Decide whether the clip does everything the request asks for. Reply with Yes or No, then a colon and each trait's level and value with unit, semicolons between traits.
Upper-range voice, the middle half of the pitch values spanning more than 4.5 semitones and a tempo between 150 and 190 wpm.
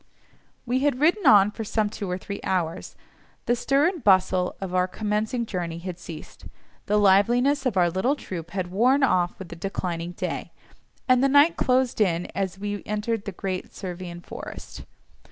Yes: high, 200 Hz; average, 5.2 semitones; average, 175 wpm